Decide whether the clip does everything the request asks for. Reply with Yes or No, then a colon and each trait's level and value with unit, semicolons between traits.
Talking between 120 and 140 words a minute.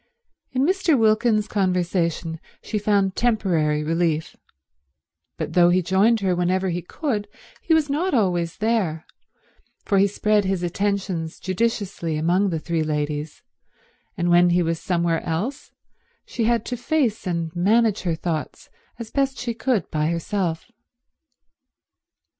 Yes: slow, 135 wpm